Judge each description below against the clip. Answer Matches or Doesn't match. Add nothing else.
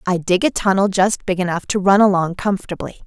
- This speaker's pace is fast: Matches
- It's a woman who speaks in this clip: Matches